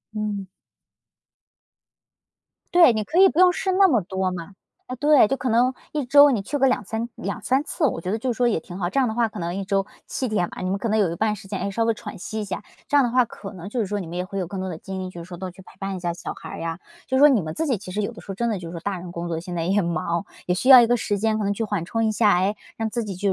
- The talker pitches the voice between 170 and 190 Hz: No, high, 205 Hz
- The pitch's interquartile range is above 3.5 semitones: Yes, average, 4.5 semitones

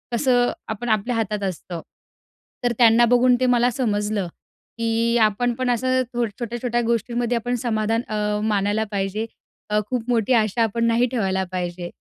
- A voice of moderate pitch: No, high, 230 Hz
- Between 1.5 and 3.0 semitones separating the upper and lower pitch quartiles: Yes, narrow, 2.5 semitones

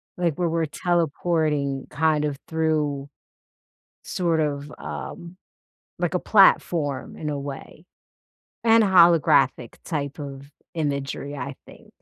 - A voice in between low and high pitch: Yes, medium, 150 Hz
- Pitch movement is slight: No, average, 3.2 semitones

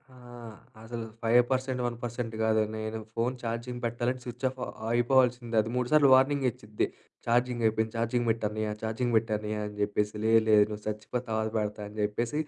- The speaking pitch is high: No, low, 115 Hz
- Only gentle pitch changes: Yes, narrow, 2.0 semitones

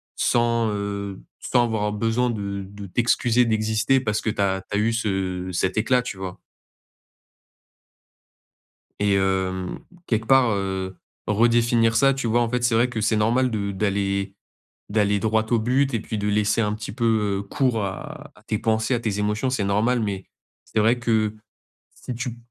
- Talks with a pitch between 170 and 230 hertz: No, low, 110 Hz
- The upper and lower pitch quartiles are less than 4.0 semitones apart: Yes, average, 2.8 semitones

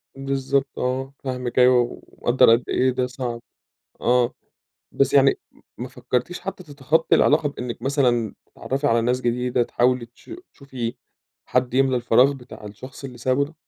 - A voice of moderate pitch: No, low, 130 Hz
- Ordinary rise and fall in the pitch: No, narrow, 2.0 semitones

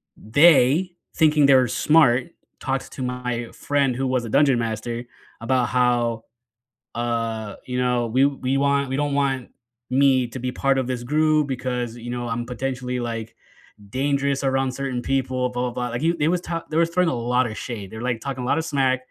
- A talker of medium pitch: No, low, 130 Hz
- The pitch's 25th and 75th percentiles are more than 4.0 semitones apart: No, narrow, 2.4 semitones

